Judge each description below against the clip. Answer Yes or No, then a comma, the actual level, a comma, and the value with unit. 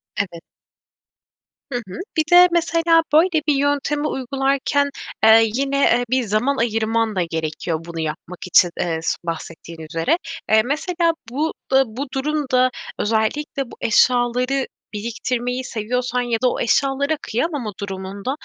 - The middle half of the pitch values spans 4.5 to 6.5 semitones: Yes, average, 4.9 semitones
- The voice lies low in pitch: No, high, 245 Hz